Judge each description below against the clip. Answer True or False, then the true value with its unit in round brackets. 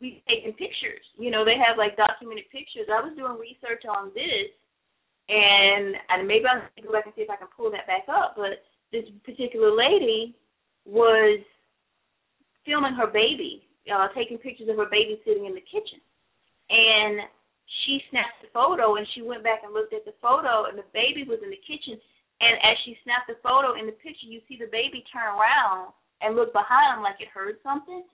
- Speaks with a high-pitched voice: True (230 Hz)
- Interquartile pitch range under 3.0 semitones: False (4.4 semitones)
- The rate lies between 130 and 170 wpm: False (195 wpm)